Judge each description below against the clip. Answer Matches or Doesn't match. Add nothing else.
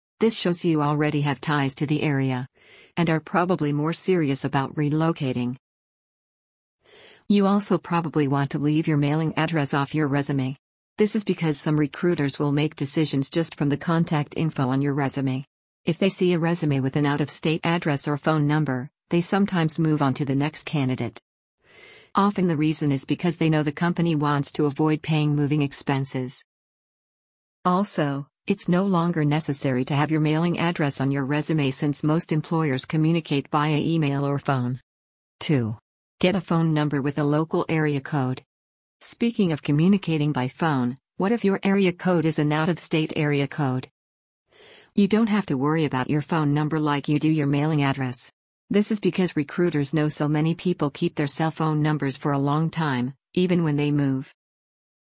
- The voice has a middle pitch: Matches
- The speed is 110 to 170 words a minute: Doesn't match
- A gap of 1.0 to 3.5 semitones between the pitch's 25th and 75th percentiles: Matches